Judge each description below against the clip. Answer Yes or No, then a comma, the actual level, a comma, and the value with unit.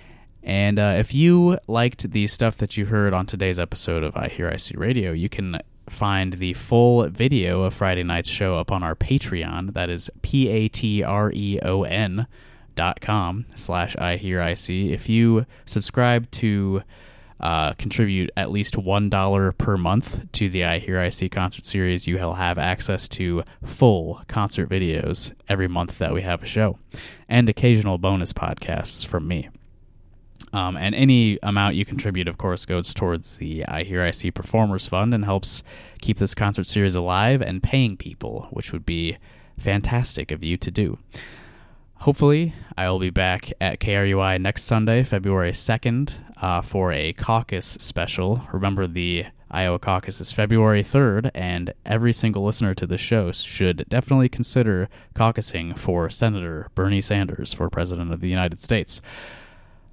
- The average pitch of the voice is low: Yes, low, 100 Hz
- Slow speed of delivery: No, average, 165 wpm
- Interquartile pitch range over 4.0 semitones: No, average, 3.6 semitones